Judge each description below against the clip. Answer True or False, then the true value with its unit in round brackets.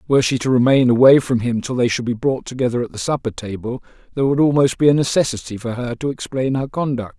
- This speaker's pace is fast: True (240 wpm)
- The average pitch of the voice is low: True (125 Hz)